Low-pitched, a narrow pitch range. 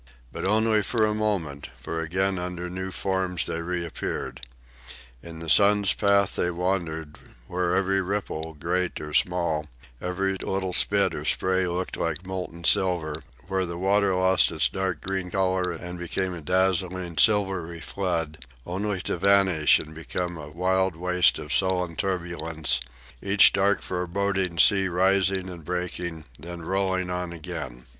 Yes: very low, 90 Hz; narrow, 2.2 semitones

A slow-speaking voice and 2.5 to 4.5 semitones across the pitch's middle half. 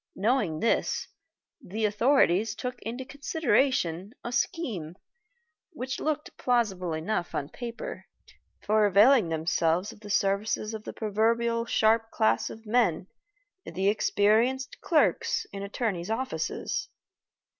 Yes: slow, 115 wpm; average, 4.0 semitones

